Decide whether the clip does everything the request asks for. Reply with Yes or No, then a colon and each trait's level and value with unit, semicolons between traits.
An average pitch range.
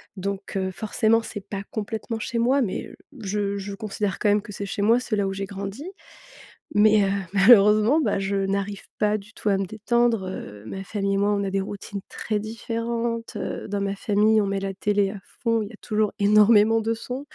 No: narrow, 2.1 semitones